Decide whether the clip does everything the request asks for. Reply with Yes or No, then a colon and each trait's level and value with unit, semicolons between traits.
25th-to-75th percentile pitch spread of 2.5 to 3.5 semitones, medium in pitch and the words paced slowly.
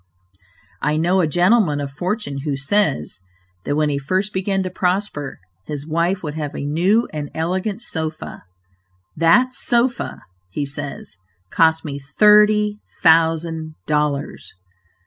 No: average, 4.8 semitones; medium, 160 Hz; slow, 130 wpm